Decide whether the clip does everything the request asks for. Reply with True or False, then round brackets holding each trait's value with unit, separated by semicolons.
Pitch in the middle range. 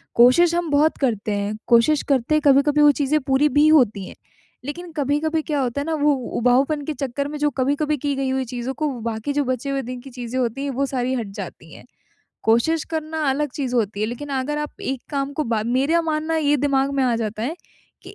False (275 Hz)